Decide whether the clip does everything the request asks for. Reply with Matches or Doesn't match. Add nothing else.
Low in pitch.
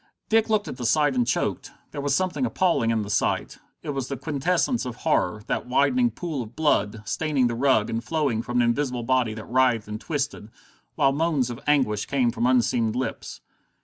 Matches